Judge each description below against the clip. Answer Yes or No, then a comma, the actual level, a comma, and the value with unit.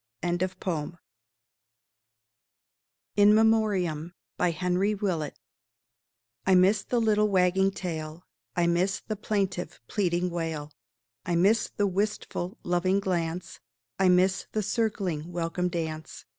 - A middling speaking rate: No, slow, 105 wpm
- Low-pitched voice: No, medium, 180 Hz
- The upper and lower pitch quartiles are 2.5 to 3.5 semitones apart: Yes, average, 3.2 semitones